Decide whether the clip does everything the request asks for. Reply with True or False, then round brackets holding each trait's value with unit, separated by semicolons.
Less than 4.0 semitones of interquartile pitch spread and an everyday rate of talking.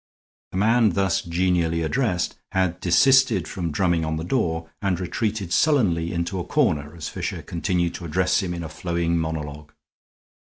True (2.7 semitones; 160 wpm)